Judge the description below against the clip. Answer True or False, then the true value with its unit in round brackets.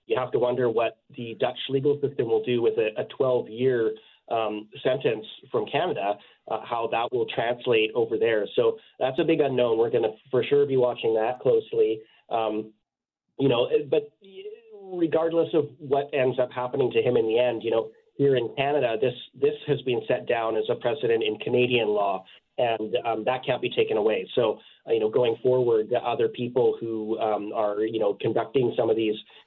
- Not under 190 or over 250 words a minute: True (195 wpm)